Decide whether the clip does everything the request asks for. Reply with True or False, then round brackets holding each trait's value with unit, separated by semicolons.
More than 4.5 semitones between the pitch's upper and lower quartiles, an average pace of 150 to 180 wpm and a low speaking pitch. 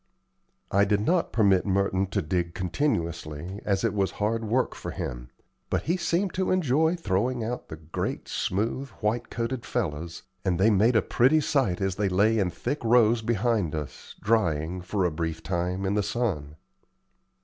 True (4.9 semitones; 170 wpm; 100 Hz)